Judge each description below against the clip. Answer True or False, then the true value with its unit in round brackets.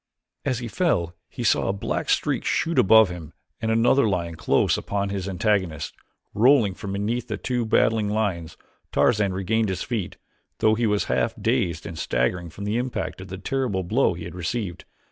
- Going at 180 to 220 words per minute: True (185 wpm)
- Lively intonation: False (4.0 semitones)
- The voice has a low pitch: True (100 Hz)